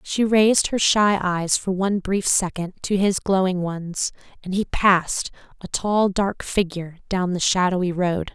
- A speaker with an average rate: Yes, average, 175 wpm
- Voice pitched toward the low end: No, high, 190 Hz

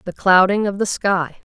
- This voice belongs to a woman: Yes, female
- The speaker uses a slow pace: No, average, 200 wpm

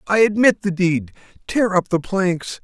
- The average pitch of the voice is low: No, medium, 185 Hz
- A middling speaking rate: Yes, average, 160 wpm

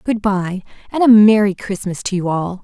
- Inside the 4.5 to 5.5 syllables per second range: Yes, 4.9 syllables/s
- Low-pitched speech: No, high, 200 Hz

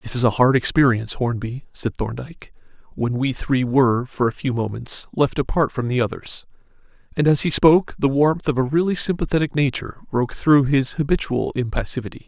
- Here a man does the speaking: Yes, male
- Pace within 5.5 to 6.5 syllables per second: Yes, 5.6 syllables/s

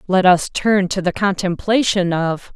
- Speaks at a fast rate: No, average, 165 wpm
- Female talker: Yes, female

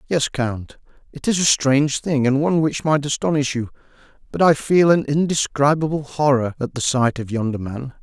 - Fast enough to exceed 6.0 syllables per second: No, 5.2 syllables/s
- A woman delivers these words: No, male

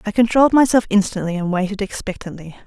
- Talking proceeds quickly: No, average, 160 wpm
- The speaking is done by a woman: Yes, female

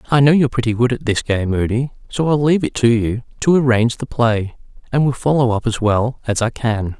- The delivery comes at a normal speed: No, fast, 240 wpm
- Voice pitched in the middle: No, low, 120 Hz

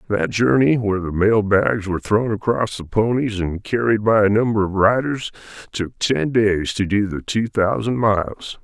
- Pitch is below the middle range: Yes, low, 105 Hz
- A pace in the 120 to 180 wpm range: No, average, 190 wpm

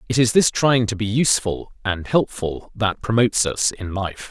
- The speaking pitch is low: Yes, low, 110 Hz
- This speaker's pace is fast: No, average, 195 wpm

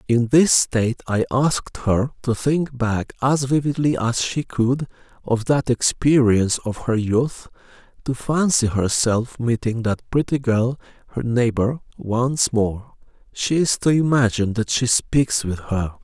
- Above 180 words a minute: No, average, 150 wpm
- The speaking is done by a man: Yes, male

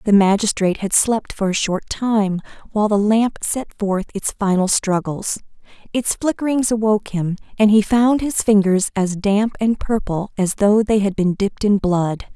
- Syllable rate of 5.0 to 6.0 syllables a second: No, 4.7 syllables/s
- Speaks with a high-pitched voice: Yes, high, 205 Hz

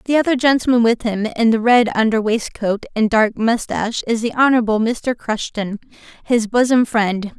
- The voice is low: No, high, 230 Hz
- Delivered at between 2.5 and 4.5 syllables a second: No, 5.0 syllables/s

